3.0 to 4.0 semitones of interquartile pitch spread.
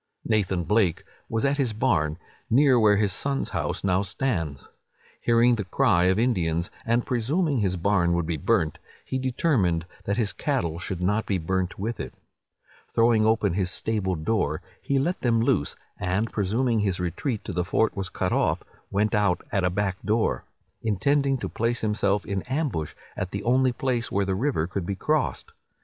No: average, 4.6 semitones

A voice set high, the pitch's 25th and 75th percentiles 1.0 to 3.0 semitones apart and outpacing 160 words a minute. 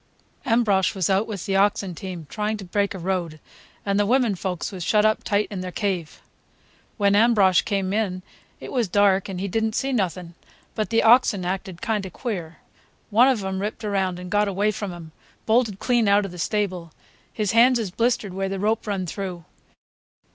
Yes: high, 200 Hz; average, 2.7 semitones; average, 200 wpm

